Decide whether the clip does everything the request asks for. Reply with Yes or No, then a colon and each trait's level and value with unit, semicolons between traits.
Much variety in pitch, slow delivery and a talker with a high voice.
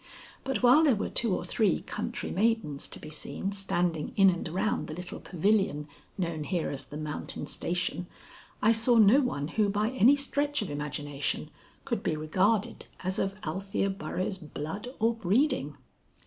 No: wide, 6.3 semitones; average, 165 wpm; high, 195 Hz